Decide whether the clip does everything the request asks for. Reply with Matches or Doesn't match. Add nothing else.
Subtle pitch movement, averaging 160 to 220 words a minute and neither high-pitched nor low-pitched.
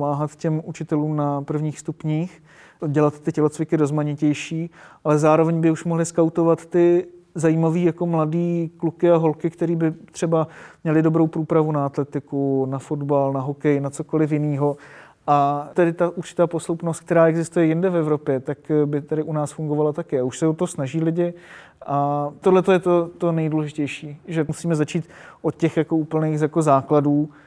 Matches